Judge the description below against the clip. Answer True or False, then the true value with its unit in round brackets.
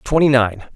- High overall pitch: False (125 Hz)